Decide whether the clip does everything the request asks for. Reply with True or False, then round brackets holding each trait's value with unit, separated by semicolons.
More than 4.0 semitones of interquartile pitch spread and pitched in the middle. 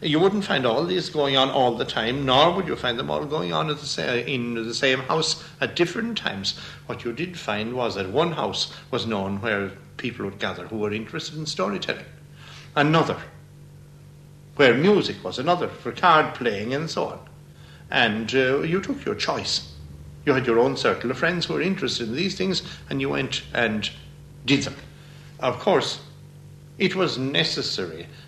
True (4.9 semitones; 145 Hz)